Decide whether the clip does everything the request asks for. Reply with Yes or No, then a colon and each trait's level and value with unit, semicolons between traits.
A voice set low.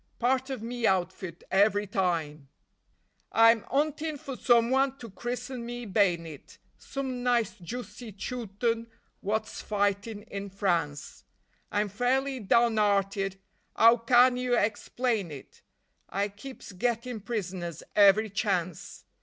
No: high, 220 Hz